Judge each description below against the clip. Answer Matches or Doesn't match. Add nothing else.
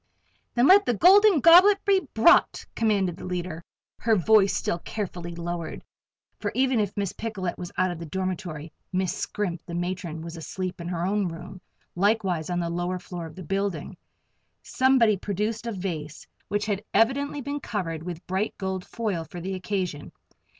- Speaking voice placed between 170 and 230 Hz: Matches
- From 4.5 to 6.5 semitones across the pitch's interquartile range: Doesn't match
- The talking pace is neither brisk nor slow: Matches